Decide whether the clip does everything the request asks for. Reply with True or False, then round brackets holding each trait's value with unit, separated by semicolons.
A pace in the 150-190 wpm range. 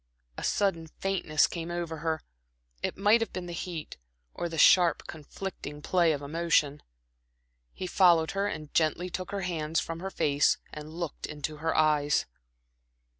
True (160 wpm)